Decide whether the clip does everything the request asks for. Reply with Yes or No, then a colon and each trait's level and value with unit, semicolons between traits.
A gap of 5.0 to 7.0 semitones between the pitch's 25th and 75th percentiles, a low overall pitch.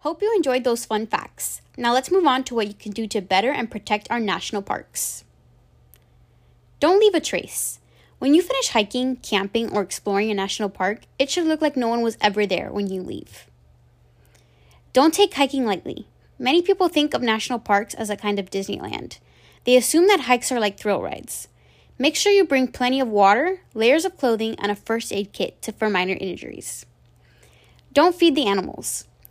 No: wide, 5.4 semitones; high, 225 Hz